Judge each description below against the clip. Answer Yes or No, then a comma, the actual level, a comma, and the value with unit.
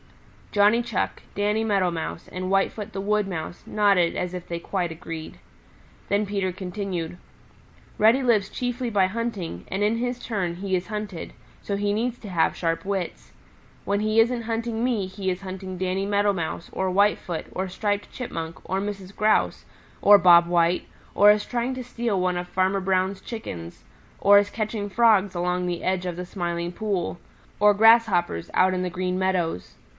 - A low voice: No, high, 195 Hz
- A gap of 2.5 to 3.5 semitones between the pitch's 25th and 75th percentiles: Yes, average, 2.8 semitones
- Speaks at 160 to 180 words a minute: Yes, average, 175 wpm